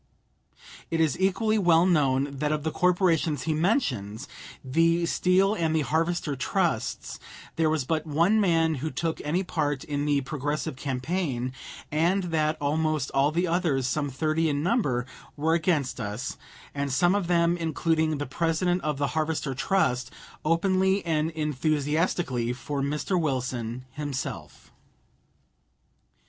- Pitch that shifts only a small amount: No, average, 3.3 semitones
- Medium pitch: Yes, medium, 155 Hz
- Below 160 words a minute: Yes, average, 140 wpm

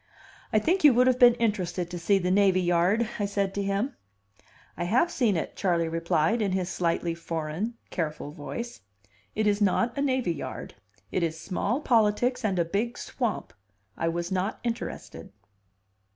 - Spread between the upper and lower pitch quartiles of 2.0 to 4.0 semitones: No, average, 5.3 semitones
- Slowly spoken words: No, average, 170 wpm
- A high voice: Yes, high, 200 Hz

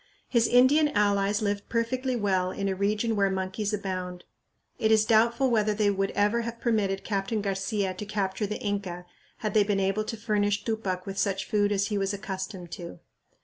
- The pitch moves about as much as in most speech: No, narrow, 2.0 semitones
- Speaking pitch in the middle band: No, high, 205 Hz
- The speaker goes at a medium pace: Yes, average, 190 wpm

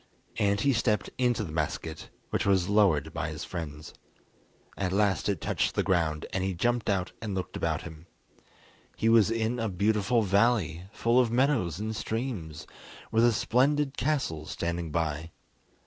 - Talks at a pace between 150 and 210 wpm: Yes, average, 165 wpm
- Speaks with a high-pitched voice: No, low, 100 Hz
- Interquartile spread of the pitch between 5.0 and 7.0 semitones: Yes, wide, 5.5 semitones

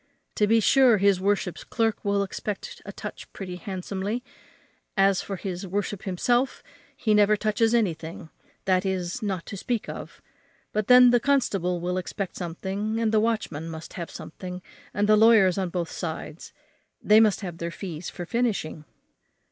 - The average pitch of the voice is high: Yes, high, 195 Hz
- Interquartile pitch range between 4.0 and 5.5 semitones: No, average, 3.2 semitones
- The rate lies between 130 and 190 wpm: Yes, average, 165 wpm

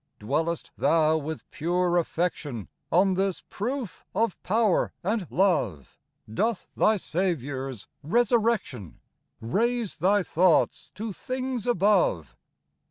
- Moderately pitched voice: Yes, medium, 180 Hz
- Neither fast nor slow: No, slow, 100 wpm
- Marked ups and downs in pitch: Yes, wide, 5.8 semitones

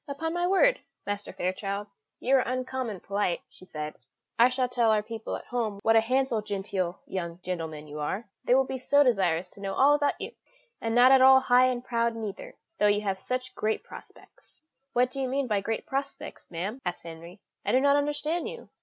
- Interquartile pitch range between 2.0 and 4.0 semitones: No, average, 5.1 semitones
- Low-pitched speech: No, high, 230 Hz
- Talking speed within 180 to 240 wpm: Yes, fast, 205 wpm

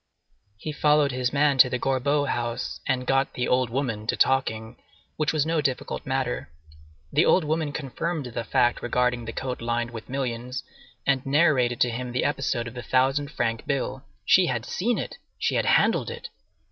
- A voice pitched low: Yes, low, 130 Hz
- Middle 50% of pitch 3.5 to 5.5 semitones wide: No, average, 3.0 semitones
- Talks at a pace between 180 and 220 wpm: Yes, average, 185 wpm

